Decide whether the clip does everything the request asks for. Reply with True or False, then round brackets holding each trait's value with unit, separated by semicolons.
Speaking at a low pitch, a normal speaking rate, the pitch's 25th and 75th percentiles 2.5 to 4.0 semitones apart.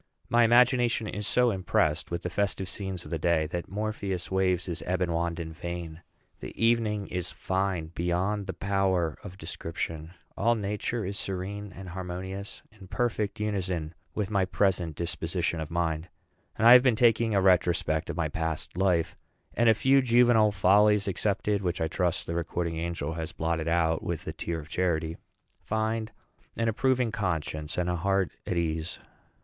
True (95 Hz; 170 wpm; 3.7 semitones)